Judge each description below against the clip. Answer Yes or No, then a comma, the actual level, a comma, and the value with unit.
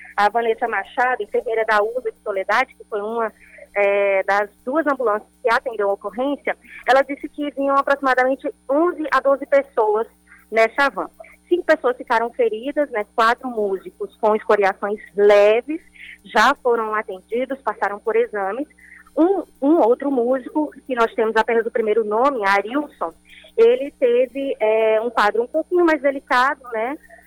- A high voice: Yes, high, 240 Hz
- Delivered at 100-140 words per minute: No, average, 150 wpm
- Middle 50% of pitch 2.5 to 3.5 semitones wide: No, average, 4.7 semitones